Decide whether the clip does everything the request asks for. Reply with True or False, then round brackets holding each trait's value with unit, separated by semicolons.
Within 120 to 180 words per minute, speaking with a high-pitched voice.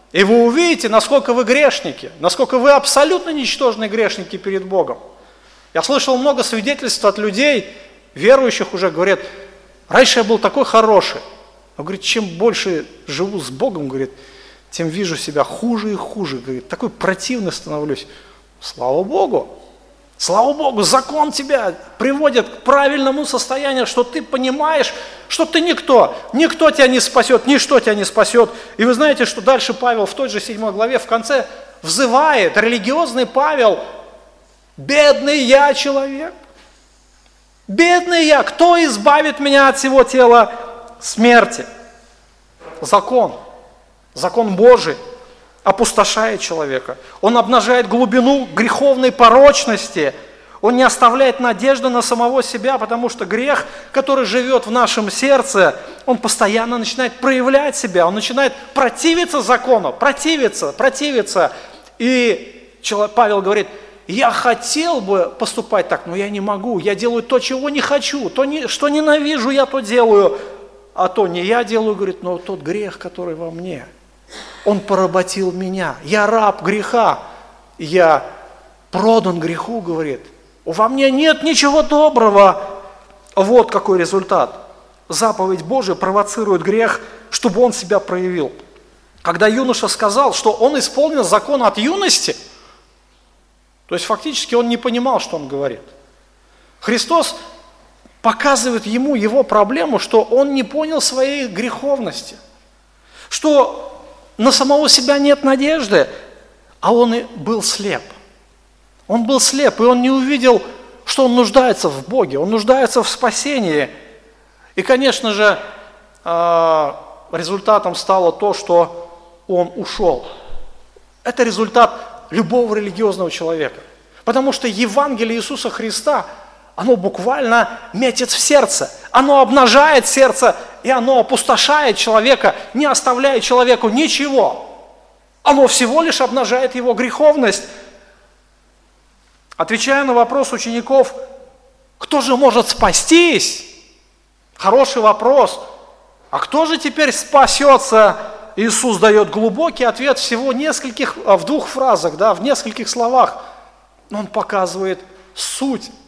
True (125 wpm; 240 Hz)